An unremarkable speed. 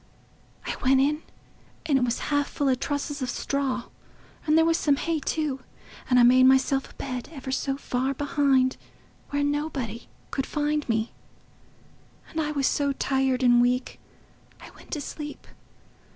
Yes: average, 165 wpm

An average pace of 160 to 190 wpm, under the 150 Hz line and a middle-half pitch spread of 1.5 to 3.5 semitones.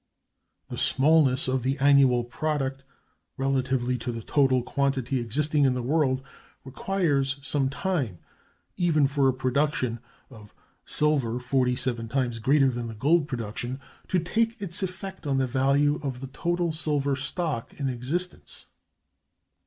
No: average, 140 wpm; low, 135 Hz; average, 3.1 semitones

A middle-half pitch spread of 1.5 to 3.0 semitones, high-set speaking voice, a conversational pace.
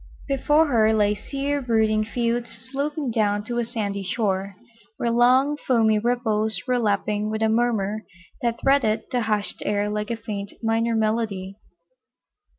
Yes: narrow, 2.4 semitones; high, 225 Hz; average, 150 wpm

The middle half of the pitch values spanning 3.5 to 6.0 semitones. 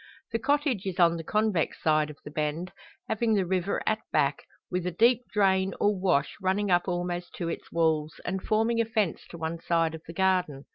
Yes: average, 4.0 semitones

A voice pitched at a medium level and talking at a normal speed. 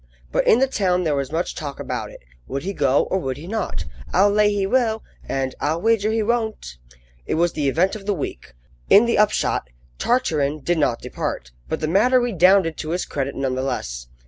No: medium, 175 Hz; fast, 210 wpm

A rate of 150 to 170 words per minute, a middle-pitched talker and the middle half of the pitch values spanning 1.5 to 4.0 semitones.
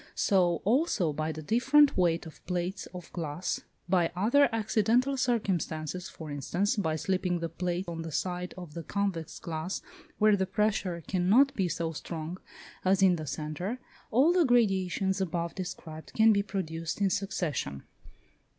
Yes: average, 155 wpm; medium, 180 Hz; average, 3.7 semitones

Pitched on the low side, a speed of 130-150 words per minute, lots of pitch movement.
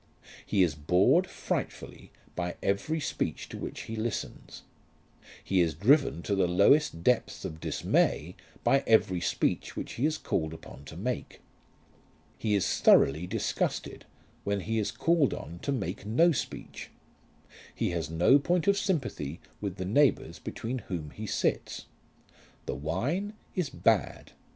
Yes: low, 100 Hz; average, 145 wpm; wide, 8.1 semitones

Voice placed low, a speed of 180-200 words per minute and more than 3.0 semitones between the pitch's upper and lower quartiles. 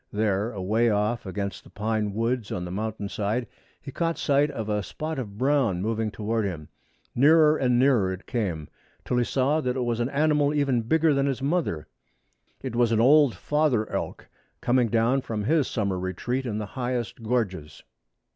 Yes: low, 115 Hz; average, 185 wpm; average, 4.6 semitones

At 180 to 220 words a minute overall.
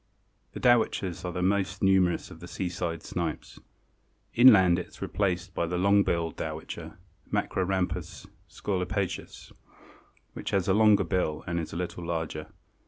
No: average, 145 wpm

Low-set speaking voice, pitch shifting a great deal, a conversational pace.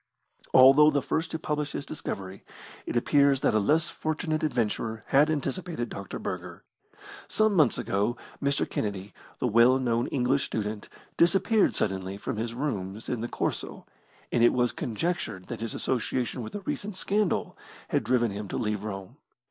Yes: low, 125 Hz; wide, 5.9 semitones; average, 165 wpm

